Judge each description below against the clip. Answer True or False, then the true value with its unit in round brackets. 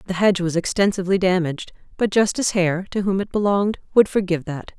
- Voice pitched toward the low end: False (190 Hz)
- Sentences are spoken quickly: False (190 wpm)